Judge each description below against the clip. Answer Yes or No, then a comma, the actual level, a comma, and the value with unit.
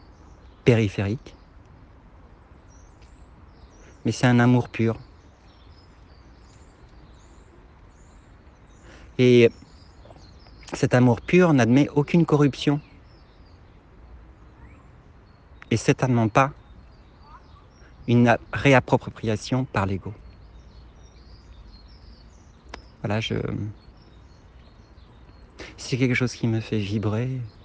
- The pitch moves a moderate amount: No, wide, 5.8 semitones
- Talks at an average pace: No, slow, 65 wpm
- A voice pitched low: Yes, low, 100 Hz